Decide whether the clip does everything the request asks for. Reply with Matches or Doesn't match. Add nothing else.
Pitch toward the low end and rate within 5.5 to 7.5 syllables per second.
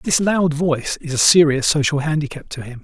Doesn't match